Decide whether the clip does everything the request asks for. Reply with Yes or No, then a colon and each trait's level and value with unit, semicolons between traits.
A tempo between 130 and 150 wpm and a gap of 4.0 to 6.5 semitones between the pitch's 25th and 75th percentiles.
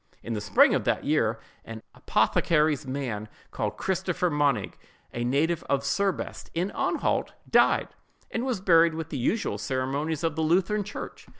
Yes: average, 145 wpm; average, 5.2 semitones